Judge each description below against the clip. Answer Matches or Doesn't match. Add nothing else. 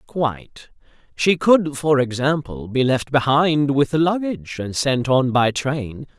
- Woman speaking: Doesn't match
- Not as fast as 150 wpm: Matches